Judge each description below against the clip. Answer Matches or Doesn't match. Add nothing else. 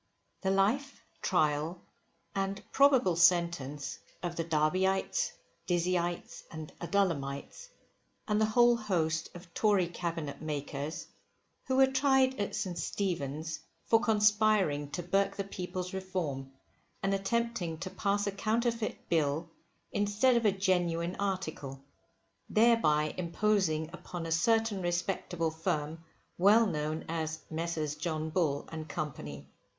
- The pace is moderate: Doesn't match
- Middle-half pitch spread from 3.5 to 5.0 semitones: Matches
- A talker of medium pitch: Matches